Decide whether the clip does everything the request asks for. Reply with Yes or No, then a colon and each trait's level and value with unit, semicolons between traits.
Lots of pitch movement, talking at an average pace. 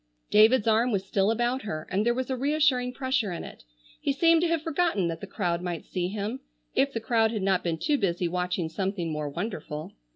No: wide, 6.4 semitones; fast, 215 wpm